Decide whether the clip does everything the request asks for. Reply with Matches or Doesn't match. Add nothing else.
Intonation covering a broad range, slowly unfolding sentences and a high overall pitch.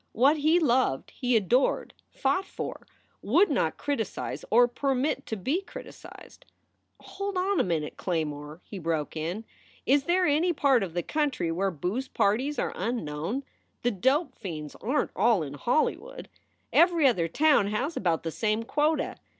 Doesn't match